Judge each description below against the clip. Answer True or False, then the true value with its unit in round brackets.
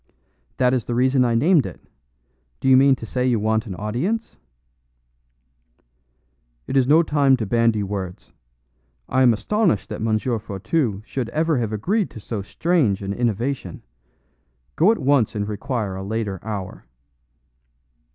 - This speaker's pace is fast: False (150 wpm)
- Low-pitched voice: True (120 Hz)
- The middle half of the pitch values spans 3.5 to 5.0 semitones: True (4.5 semitones)